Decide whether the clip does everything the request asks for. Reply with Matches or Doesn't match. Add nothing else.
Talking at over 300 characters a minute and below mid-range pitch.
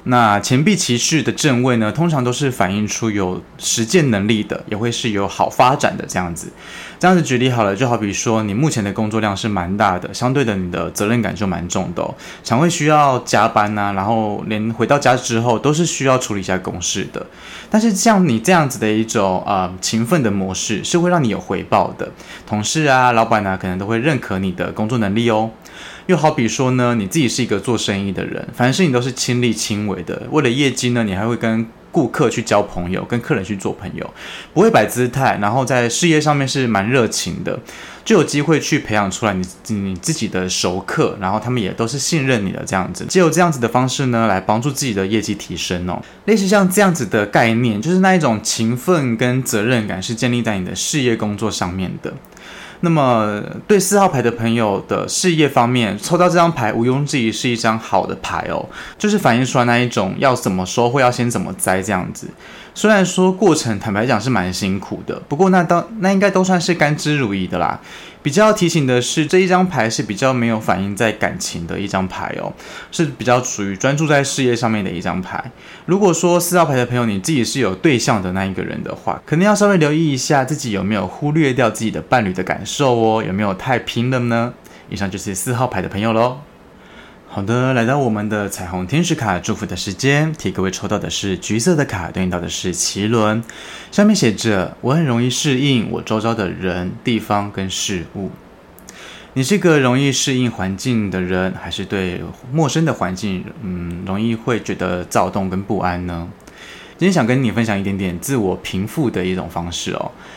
Matches